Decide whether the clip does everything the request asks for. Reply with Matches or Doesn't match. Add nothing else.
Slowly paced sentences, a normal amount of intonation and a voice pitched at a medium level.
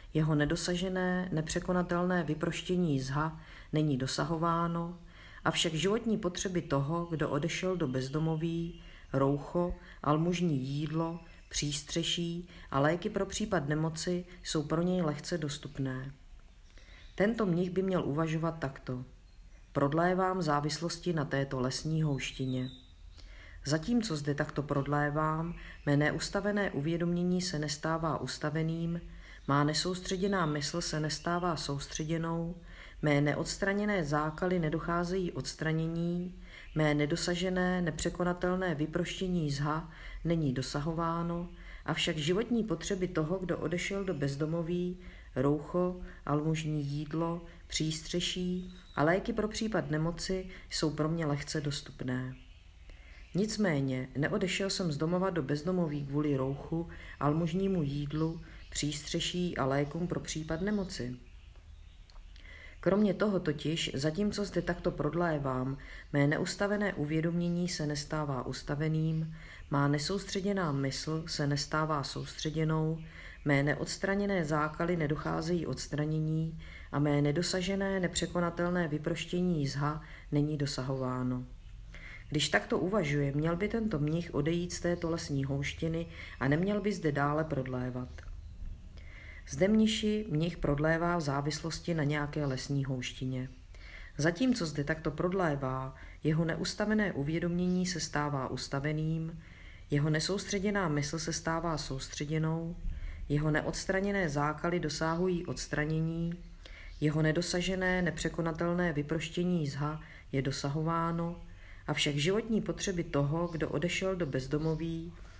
Matches